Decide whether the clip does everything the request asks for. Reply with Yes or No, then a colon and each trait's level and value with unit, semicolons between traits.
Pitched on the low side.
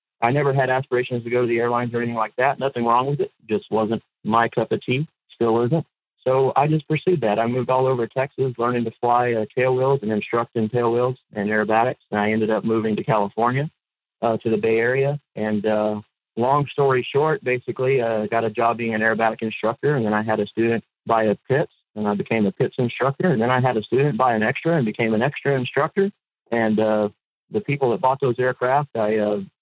Yes: low, 120 Hz